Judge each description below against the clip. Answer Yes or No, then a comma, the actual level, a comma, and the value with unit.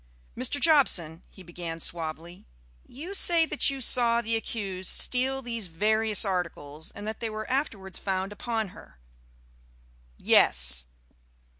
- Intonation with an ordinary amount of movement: No, wide, 5.7 semitones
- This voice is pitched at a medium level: No, high, 210 Hz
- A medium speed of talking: No, slow, 130 wpm